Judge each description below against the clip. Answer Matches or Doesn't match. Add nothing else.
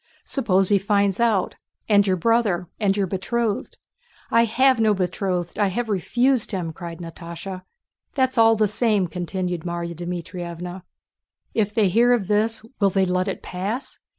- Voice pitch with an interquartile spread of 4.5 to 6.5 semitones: Doesn't match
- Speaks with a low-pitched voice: Doesn't match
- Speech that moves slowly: Doesn't match